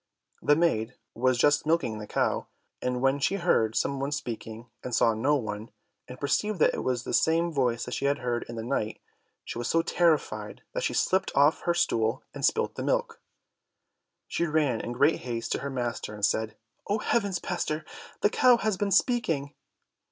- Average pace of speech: Yes, average, 195 wpm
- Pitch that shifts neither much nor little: No, wide, 5.9 semitones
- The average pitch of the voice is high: No, medium, 140 Hz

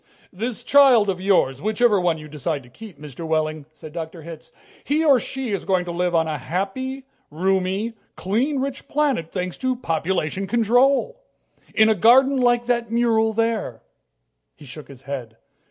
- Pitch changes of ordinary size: No, wide, 7.1 semitones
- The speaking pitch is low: No, high, 195 Hz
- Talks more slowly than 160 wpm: No, average, 170 wpm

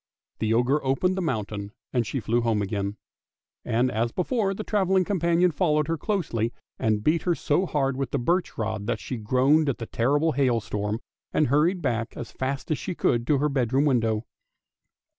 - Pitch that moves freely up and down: Yes, wide, 6.0 semitones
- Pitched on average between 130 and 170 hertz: Yes, low, 135 Hz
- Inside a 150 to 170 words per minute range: No, average, 185 wpm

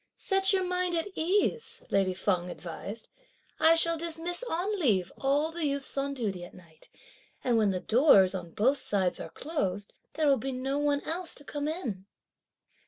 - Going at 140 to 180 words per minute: Yes, average, 175 wpm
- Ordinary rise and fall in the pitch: No, wide, 8.8 semitones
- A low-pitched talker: No, very high, 280 Hz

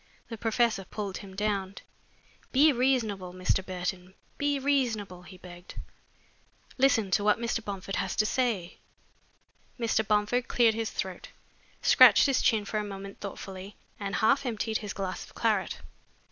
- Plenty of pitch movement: No, average, 3.4 semitones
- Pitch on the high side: Yes, high, 210 Hz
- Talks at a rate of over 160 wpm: No, average, 145 wpm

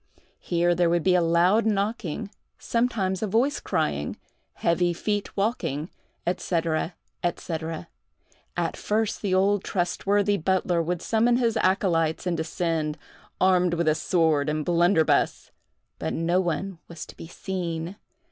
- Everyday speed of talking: No, slow, 125 wpm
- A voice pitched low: No, medium, 180 Hz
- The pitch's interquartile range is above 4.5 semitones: No, average, 3.2 semitones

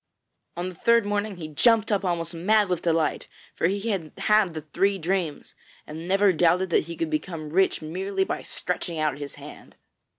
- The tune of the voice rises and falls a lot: No, average, 3.6 semitones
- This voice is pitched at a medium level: Yes, medium, 180 Hz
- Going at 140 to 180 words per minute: No, average, 190 wpm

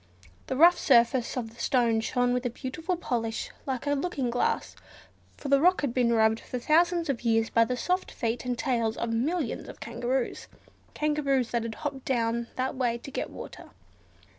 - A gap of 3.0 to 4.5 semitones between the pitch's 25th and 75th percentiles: Yes, average, 3.3 semitones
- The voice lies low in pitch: No, very high, 250 Hz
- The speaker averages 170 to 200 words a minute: Yes, average, 190 wpm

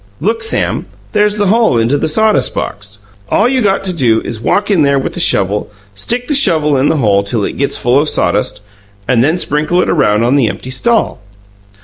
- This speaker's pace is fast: Yes, fast, 215 wpm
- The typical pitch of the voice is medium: Yes, medium, 145 Hz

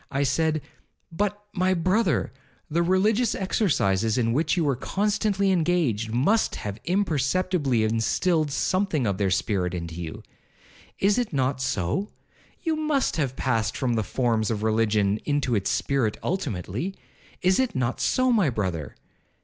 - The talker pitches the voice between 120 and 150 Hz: Yes, medium, 140 Hz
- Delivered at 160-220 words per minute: No, average, 140 wpm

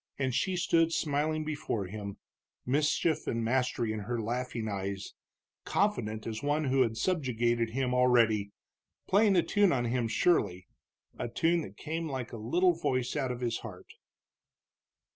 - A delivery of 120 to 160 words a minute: Yes, average, 155 wpm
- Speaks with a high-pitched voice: No, low, 125 Hz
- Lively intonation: Yes, wide, 5.7 semitones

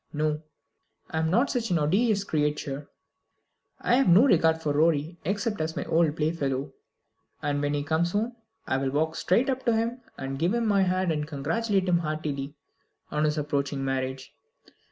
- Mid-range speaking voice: Yes, medium, 160 Hz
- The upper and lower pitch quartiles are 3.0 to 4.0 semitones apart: No, average, 5.1 semitones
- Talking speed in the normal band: Yes, average, 175 wpm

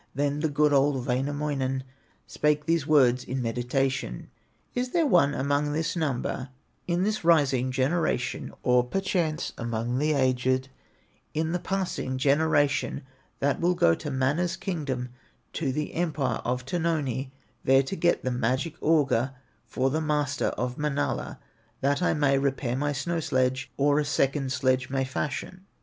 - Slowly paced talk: No, average, 150 wpm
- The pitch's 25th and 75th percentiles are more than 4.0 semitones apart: No, average, 3.0 semitones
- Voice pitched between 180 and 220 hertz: No, medium, 140 Hz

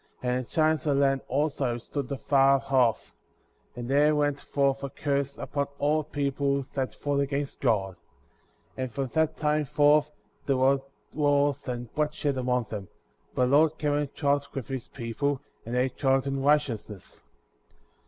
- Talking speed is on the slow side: No, average, 165 wpm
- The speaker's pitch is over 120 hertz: Yes, medium, 140 Hz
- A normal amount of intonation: No, narrow, 2.0 semitones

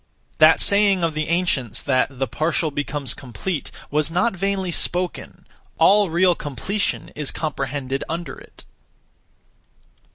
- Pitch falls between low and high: Yes, medium, 160 Hz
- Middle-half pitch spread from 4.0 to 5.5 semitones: Yes, average, 4.6 semitones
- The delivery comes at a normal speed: No, slow, 125 wpm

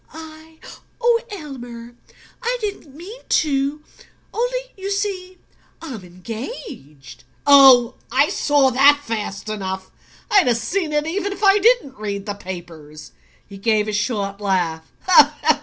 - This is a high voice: Yes, very high, 270 Hz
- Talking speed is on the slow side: Yes, slow, 130 wpm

